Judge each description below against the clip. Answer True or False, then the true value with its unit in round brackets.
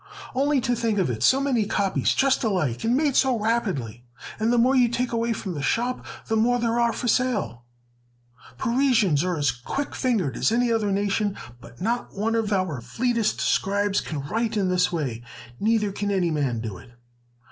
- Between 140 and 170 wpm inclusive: False (190 wpm)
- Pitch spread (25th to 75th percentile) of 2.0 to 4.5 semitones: False (5.5 semitones)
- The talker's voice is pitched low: False (215 Hz)